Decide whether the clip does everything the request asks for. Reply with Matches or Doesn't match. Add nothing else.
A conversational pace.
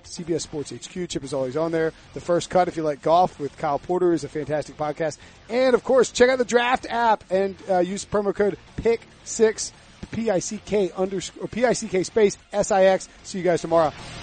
Doesn't match